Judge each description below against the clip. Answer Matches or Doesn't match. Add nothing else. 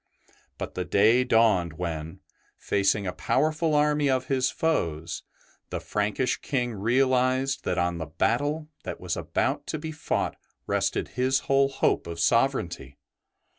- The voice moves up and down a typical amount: Doesn't match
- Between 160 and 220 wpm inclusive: Doesn't match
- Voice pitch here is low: Matches